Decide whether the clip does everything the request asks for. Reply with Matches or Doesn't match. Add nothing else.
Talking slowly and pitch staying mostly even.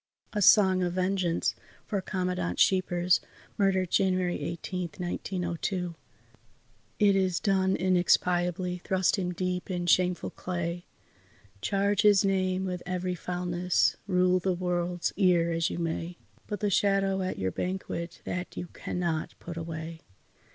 Matches